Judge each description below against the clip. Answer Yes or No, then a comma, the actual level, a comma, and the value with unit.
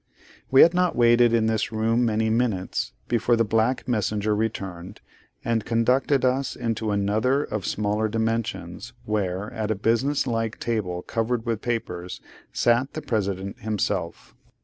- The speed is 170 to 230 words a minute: No, average, 145 wpm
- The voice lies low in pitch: Yes, low, 110 Hz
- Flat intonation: Yes, narrow, 2.2 semitones